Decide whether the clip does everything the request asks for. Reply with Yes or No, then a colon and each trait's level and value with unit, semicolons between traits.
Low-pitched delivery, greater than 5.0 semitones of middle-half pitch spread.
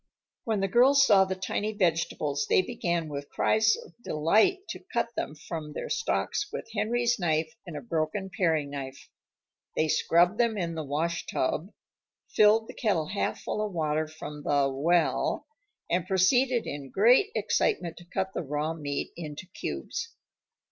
No: medium, 175 Hz; wide, 5.6 semitones